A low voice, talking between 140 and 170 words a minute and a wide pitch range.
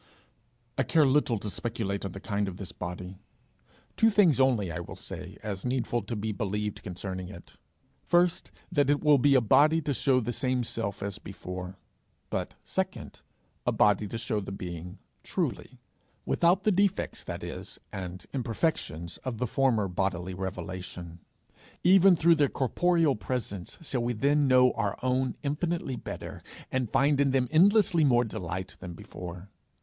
Yes: low, 115 Hz; average, 165 wpm; wide, 6.7 semitones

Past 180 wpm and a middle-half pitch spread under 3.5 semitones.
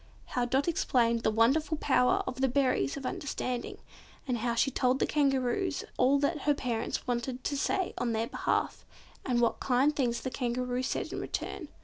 Yes: average, 190 wpm; narrow, 2.6 semitones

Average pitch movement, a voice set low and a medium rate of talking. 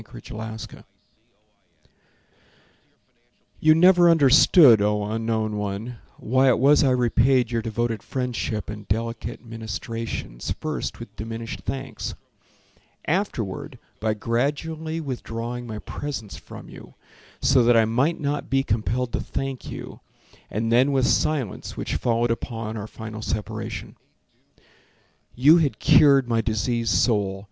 No: average, 3.6 semitones; low, 115 Hz; slow, 125 wpm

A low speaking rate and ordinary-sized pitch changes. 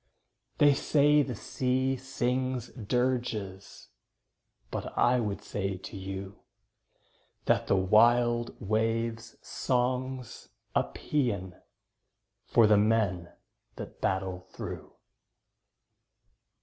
Yes: slow, 90 wpm; average, 4.3 semitones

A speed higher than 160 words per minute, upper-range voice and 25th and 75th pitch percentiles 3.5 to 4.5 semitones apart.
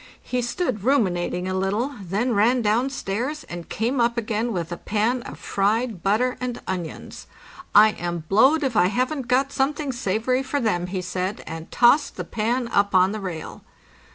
No: average, 180 wpm; high, 220 Hz; average, 5.0 semitones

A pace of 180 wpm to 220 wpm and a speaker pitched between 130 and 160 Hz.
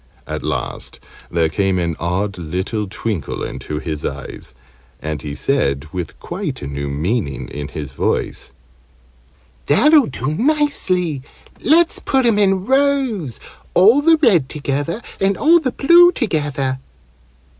No: slow, 135 wpm; medium, 140 Hz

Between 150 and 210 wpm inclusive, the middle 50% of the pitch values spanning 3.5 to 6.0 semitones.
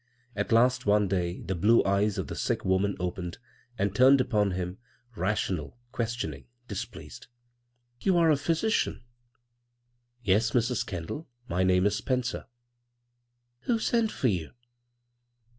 No: average, 140 wpm; average, 4.5 semitones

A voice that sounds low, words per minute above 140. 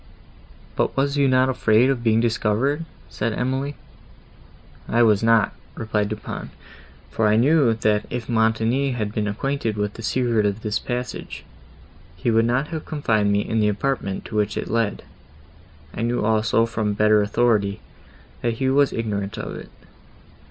Yes: low, 115 Hz; average, 165 wpm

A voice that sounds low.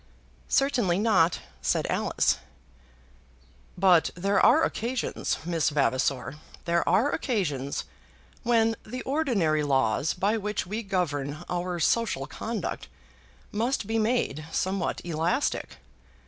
No: medium, 185 Hz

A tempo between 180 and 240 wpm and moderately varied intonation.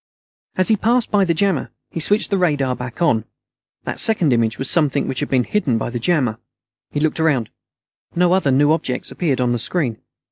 No: fast, 205 wpm; wide, 6.1 semitones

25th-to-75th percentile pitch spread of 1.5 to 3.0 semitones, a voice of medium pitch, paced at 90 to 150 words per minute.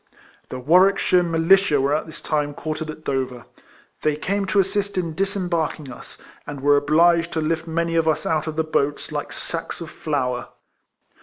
No: average, 2.7 semitones; medium, 160 Hz; average, 175 wpm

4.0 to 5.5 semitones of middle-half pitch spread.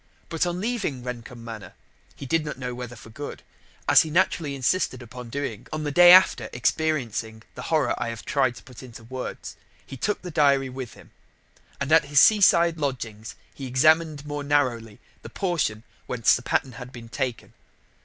Yes: average, 4.5 semitones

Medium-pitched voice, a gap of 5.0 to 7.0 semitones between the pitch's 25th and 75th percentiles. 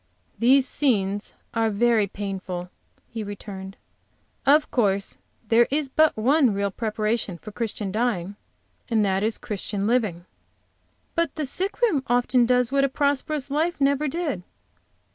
No: high, 230 Hz; wide, 5.4 semitones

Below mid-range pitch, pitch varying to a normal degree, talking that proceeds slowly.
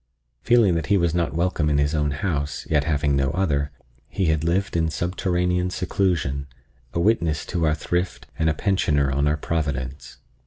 No: very low, 80 Hz; average, 3.6 semitones; average, 180 wpm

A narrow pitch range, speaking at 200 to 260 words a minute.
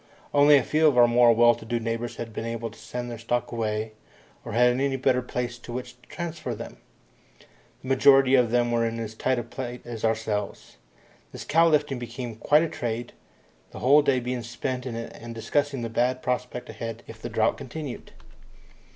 Yes: narrow, 2.0 semitones; fast, 205 wpm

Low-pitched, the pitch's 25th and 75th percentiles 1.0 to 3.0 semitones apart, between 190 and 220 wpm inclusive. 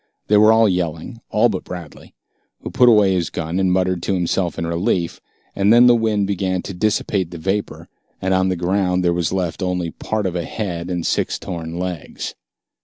Yes: very low, 95 Hz; average, 2.7 semitones; average, 200 wpm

